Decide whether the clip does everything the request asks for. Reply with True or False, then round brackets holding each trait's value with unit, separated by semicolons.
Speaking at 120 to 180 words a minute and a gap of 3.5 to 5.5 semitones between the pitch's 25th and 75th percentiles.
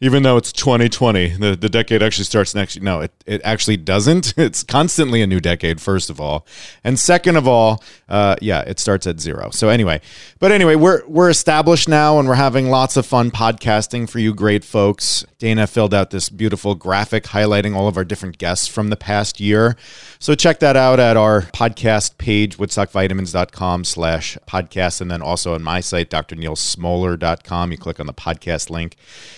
False (190 wpm; 4.8 semitones)